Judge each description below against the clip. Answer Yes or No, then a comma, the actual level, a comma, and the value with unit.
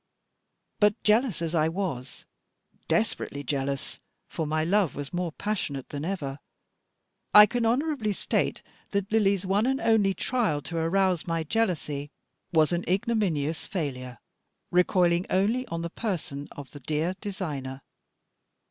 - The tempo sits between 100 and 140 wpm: Yes, slow, 135 wpm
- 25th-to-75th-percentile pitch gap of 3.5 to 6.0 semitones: Yes, wide, 5.6 semitones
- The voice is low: No, medium, 175 Hz